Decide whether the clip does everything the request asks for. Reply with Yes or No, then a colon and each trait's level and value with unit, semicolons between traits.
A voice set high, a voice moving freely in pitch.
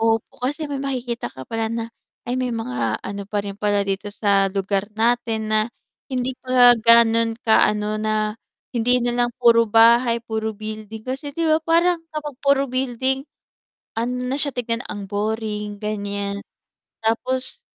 No: high, 225 Hz; average, 3.1 semitones